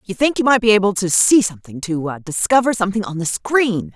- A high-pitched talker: Yes, high, 200 Hz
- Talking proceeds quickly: Yes, fast, 230 wpm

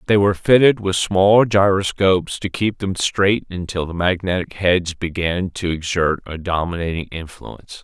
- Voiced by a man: Yes, male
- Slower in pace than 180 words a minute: Yes, average, 155 wpm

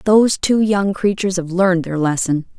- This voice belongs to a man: No, female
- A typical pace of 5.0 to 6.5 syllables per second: Yes, 5.5 syllables/s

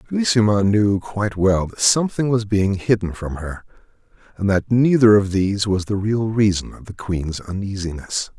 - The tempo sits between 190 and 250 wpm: No, average, 165 wpm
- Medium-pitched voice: No, low, 100 Hz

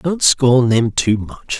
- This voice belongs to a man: Yes, male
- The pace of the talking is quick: No, average, 190 wpm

